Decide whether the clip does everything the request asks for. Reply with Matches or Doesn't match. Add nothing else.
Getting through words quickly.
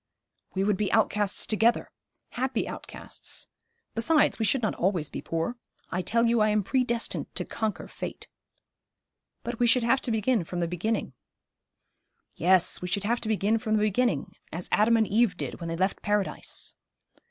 Doesn't match